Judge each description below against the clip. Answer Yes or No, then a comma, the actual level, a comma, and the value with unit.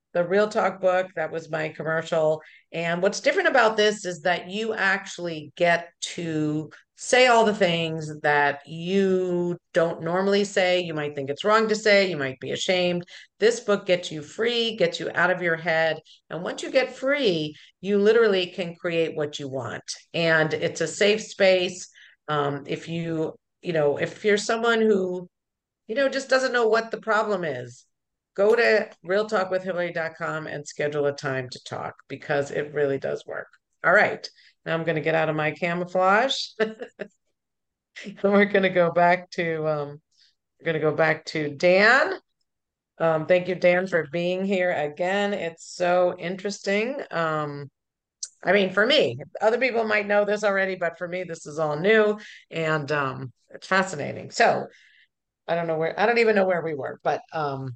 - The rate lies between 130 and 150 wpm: No, average, 175 wpm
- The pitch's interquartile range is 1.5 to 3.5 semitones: No, average, 4.3 semitones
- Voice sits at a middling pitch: Yes, medium, 175 Hz